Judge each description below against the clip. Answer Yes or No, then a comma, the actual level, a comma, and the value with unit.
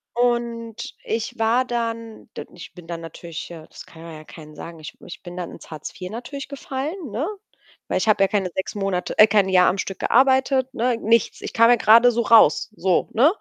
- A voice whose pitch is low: No, high, 220 Hz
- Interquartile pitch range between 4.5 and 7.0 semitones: Yes, average, 4.9 semitones